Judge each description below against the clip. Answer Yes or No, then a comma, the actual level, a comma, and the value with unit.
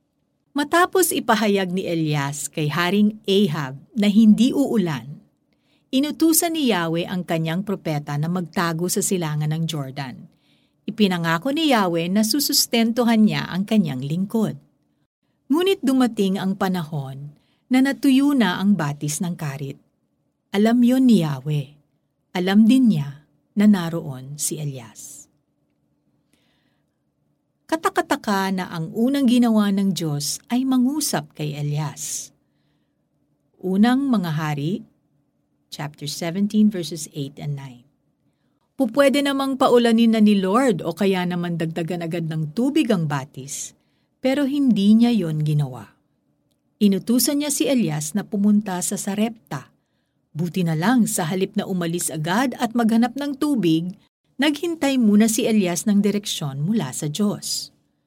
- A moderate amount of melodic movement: No, wide, 7.2 semitones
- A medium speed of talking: Yes, average, 125 wpm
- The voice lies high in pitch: Yes, high, 195 Hz